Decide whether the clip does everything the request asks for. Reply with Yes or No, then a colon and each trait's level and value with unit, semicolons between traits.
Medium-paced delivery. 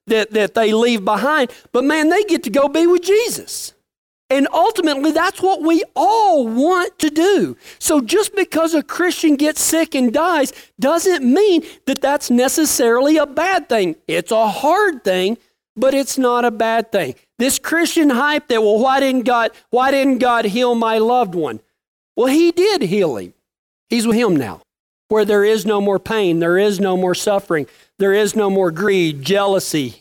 Yes: average, 180 wpm